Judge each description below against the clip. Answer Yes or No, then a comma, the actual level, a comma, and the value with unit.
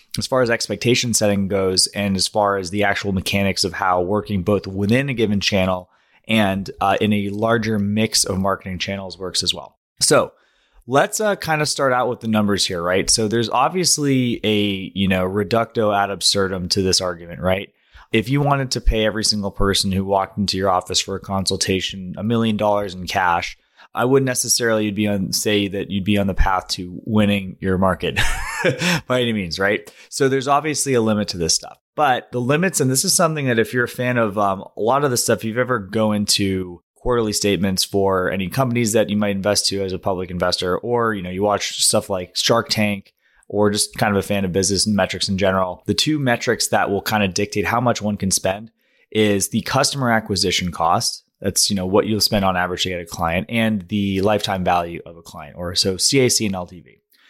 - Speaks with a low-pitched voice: Yes, low, 105 Hz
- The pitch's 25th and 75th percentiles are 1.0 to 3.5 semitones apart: Yes, average, 3.2 semitones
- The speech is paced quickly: Yes, fast, 220 wpm